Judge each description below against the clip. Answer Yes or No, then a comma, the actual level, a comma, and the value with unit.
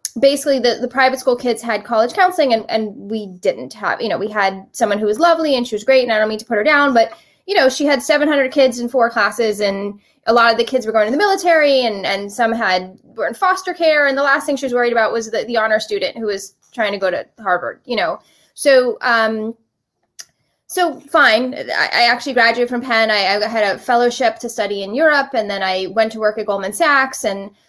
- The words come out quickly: Yes, fast, 245 wpm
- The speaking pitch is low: No, high, 230 Hz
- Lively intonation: No, average, 4.1 semitones